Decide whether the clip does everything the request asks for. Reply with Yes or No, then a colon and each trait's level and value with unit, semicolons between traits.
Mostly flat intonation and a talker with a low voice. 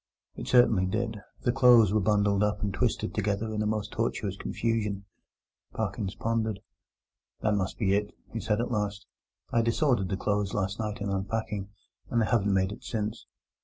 Yes: narrow, 2.1 semitones; low, 105 Hz